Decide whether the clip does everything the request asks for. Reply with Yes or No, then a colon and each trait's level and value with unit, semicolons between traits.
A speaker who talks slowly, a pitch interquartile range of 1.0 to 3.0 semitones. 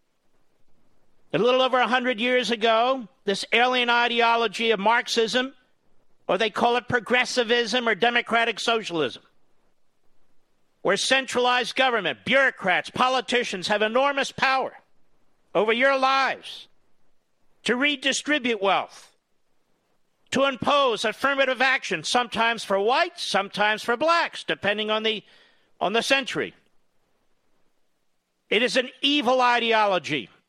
Yes: slow, 110 wpm; average, 2.7 semitones